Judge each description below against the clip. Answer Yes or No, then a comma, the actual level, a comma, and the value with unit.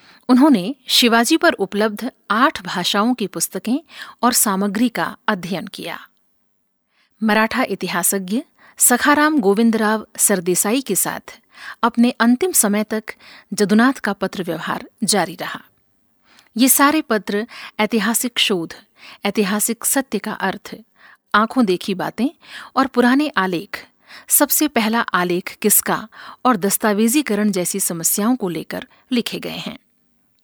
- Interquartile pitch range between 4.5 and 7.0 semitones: No, average, 3.7 semitones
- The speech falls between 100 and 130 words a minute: Yes, average, 115 wpm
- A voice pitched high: Yes, high, 220 Hz